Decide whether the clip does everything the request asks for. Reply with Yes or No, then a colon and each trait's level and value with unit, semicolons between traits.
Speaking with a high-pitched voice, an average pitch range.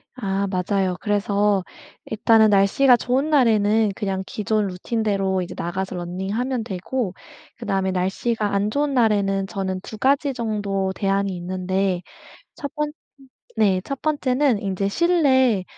Yes: high, 205 Hz; average, 3.9 semitones